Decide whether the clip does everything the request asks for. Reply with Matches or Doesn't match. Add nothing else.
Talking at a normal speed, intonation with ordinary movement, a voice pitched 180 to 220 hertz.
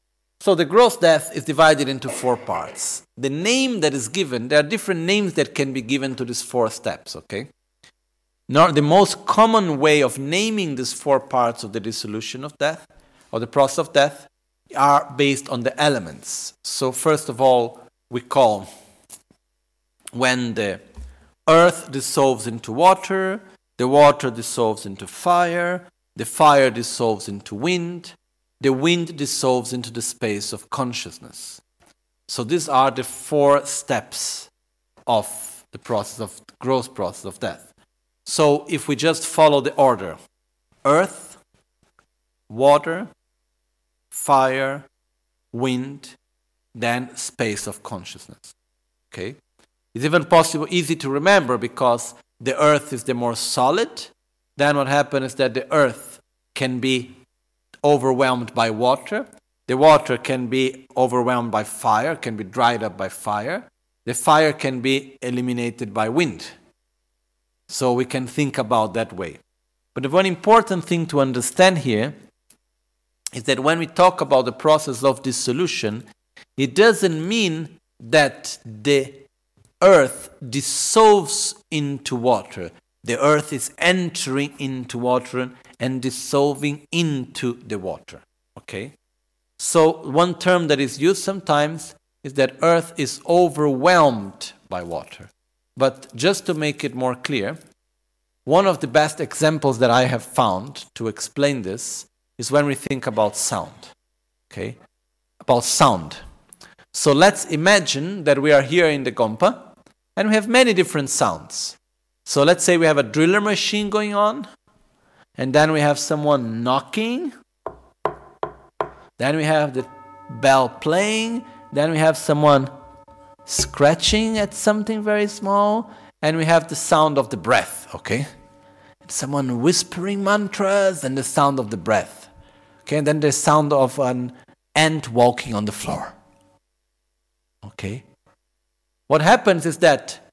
Doesn't match